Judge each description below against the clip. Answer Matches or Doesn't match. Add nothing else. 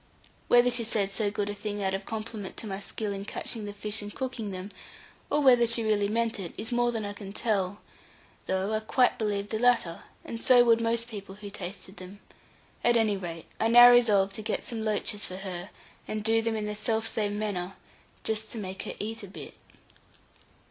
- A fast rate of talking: Matches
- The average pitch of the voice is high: Matches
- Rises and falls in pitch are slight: Matches